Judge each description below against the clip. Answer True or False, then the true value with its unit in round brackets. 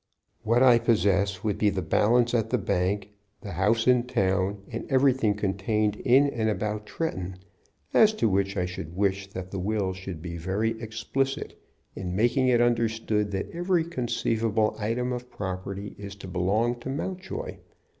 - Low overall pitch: True (105 Hz)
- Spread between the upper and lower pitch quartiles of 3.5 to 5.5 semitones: True (3.8 semitones)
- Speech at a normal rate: True (165 wpm)